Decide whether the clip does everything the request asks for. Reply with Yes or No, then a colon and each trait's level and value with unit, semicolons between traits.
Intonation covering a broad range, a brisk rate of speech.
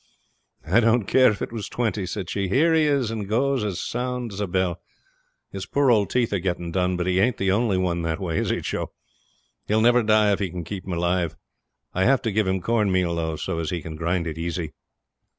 No: average, 4.6 semitones; fast, 240 wpm